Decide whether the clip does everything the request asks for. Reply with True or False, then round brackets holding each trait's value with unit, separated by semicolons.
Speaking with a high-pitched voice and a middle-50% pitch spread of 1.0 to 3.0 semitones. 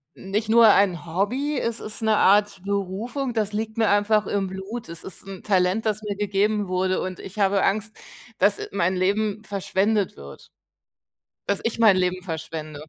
True (200 Hz; 2.4 semitones)